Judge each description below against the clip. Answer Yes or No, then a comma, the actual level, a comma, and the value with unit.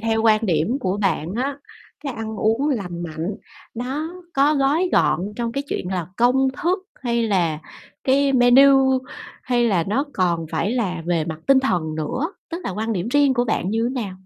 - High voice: Yes, high, 230 Hz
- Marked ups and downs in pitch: Yes, wide, 6.5 semitones